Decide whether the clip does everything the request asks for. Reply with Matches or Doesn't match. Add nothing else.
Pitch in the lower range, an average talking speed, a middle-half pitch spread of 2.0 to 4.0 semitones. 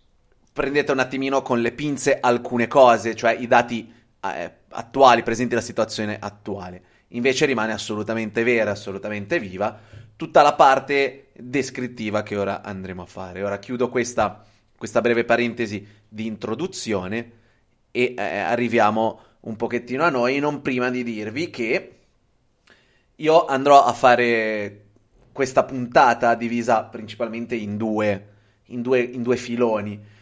Matches